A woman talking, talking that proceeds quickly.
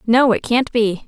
Yes: female; fast, 220 wpm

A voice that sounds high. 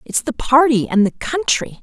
Yes: very high, 255 Hz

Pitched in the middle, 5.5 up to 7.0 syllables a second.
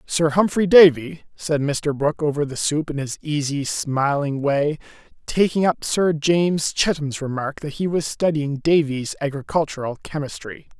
No: medium, 150 Hz; 4.5 syllables/s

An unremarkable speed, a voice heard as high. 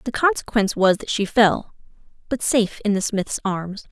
Yes: average, 170 wpm; high, 215 Hz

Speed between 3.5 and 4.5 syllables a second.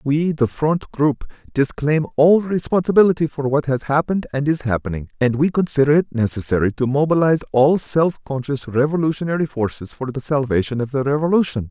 No: 5.7 syllables/s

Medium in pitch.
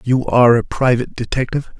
No: low, 125 Hz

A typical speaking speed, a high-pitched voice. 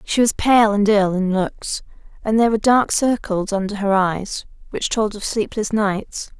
Yes: average, 190 wpm; high, 210 Hz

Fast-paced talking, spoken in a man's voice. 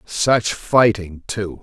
No: slow, 110 wpm; male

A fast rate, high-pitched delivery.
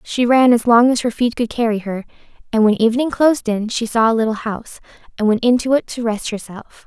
Yes: fast, 235 wpm; high, 230 Hz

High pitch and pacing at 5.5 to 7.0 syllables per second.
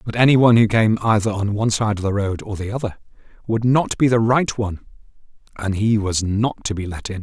No: low, 110 Hz; 5.9 syllables/s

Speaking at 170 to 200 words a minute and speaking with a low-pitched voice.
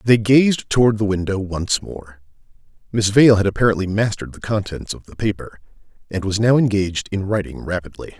Yes: average, 175 wpm; low, 100 Hz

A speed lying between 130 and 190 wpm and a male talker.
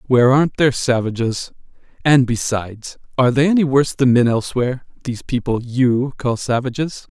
Yes: average, 150 wpm; male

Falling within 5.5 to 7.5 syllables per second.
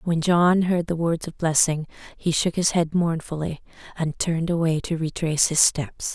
No: 4.8 syllables/s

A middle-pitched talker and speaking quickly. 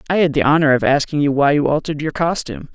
Yes: medium, 150 Hz; fast, 260 wpm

